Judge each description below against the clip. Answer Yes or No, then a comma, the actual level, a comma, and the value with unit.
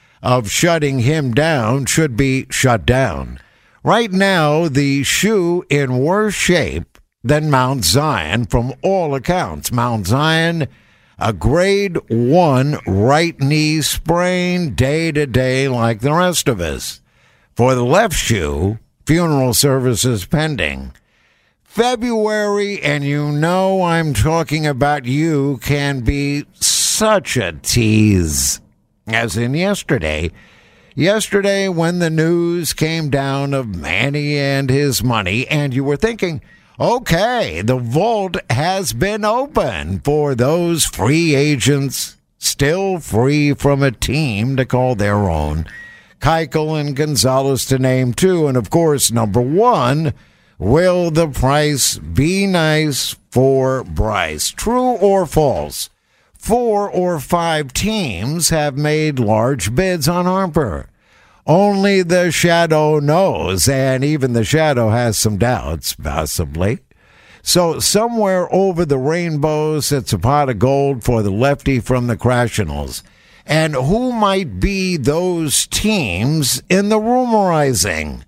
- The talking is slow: Yes, slow, 125 wpm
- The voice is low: No, medium, 145 Hz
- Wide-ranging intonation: Yes, wide, 5.8 semitones